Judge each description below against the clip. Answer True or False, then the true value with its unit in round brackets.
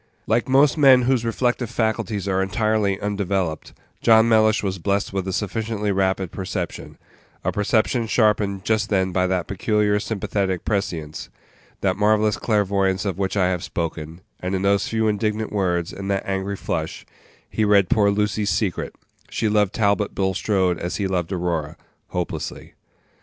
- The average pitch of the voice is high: False (100 Hz)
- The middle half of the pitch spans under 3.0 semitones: True (2.4 semitones)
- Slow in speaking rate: False (155 wpm)